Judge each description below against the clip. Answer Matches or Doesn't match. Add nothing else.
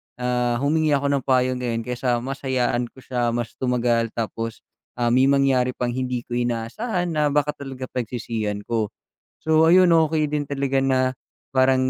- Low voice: Matches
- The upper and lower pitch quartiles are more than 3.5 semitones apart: Doesn't match